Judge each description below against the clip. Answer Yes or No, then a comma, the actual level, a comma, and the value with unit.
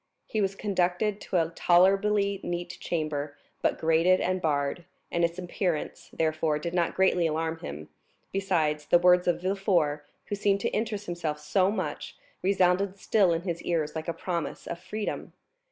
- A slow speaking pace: No, average, 165 wpm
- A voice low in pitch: No, medium, 175 Hz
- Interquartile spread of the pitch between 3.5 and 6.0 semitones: No, average, 3.0 semitones